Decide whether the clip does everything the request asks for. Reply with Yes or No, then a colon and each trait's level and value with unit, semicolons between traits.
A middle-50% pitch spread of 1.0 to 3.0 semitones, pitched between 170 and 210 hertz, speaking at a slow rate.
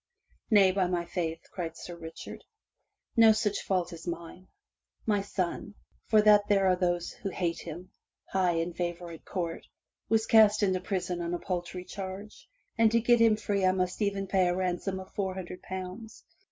No: average, 2.7 semitones; medium, 185 Hz; average, 180 wpm